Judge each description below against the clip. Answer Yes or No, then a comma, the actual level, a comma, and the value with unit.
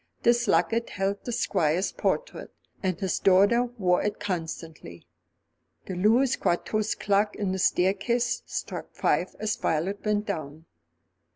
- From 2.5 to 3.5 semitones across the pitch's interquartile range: Yes, average, 3.2 semitones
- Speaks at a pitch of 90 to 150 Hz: No, high, 200 Hz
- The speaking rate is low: Yes, slow, 130 wpm